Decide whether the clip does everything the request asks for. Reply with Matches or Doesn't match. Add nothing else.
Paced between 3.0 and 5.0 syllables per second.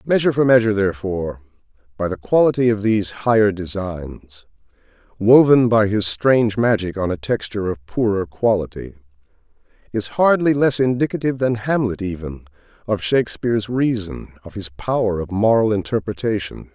Doesn't match